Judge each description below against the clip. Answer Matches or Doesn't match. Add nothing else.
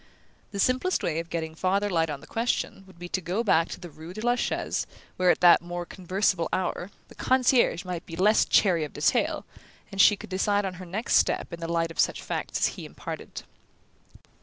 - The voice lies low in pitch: Doesn't match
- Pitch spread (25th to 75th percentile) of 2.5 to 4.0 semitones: Matches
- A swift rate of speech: Matches